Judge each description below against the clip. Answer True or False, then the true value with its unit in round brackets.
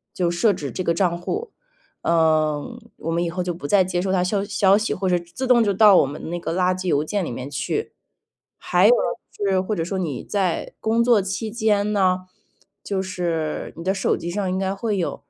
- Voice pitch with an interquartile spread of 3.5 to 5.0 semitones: False (3.1 semitones)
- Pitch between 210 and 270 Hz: False (185 Hz)